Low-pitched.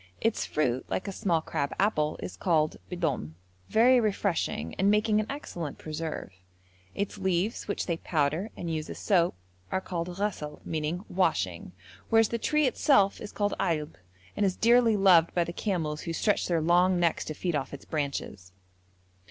No: medium, 175 Hz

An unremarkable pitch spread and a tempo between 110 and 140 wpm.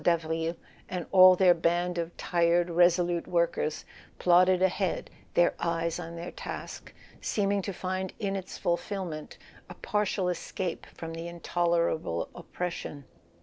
No: narrow, 1.6 semitones; slow, 135 wpm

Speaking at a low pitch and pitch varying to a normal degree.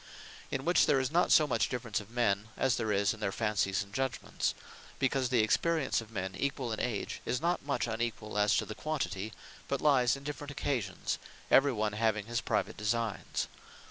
Yes: low, 115 Hz; average, 4.1 semitones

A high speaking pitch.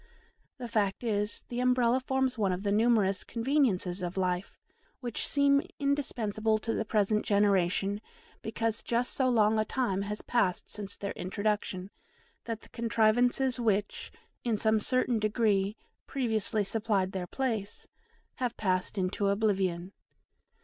Yes: high, 215 Hz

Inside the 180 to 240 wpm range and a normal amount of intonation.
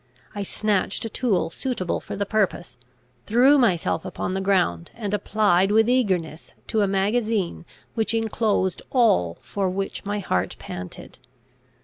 No: average, 140 wpm; average, 3.3 semitones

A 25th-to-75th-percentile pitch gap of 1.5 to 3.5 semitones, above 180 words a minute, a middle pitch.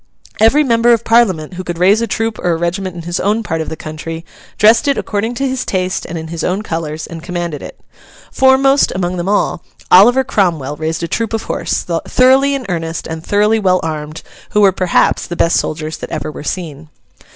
No: wide, 5.5 semitones; fast, 205 wpm; medium, 180 Hz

